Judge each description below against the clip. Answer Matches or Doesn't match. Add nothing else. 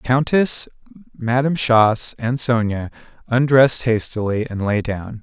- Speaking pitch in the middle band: Doesn't match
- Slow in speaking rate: Matches